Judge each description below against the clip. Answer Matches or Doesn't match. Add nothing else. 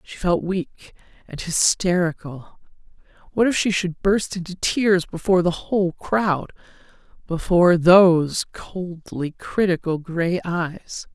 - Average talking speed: Doesn't match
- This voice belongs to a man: Doesn't match